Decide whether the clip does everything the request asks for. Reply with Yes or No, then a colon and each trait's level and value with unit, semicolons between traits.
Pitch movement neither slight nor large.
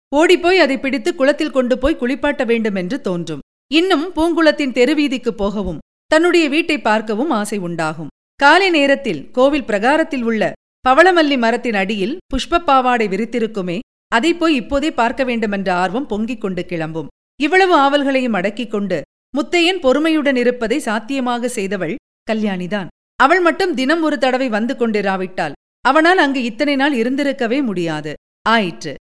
No: wide, 5.9 semitones